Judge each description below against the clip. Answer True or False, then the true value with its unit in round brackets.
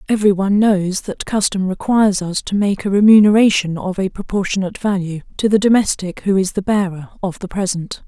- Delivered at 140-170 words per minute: False (185 wpm)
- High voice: True (195 Hz)